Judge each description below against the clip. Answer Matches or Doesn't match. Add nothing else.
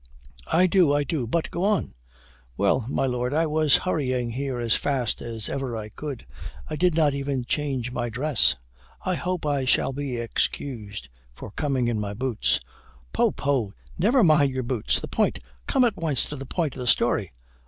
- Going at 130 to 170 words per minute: Doesn't match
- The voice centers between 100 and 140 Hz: Matches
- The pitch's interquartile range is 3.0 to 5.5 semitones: Matches